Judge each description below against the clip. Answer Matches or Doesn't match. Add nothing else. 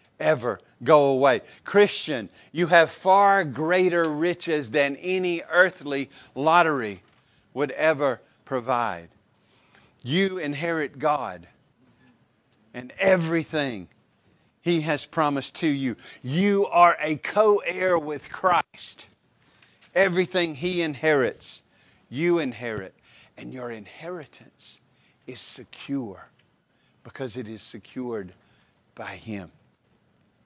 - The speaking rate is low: Matches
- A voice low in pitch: Doesn't match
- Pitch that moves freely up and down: Matches